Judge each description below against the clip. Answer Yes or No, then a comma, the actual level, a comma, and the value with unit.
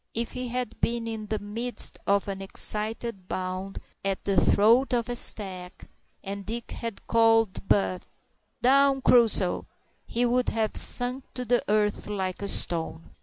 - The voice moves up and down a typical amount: Yes, average, 3.5 semitones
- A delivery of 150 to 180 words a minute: Yes, average, 155 wpm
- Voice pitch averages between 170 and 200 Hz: No, high, 220 Hz